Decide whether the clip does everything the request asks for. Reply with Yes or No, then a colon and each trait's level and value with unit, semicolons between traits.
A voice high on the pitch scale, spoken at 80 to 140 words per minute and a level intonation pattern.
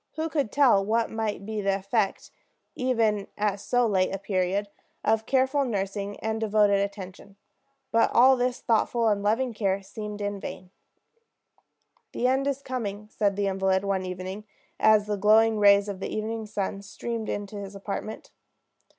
No: high, 210 Hz; average, 160 wpm; narrow, 2.3 semitones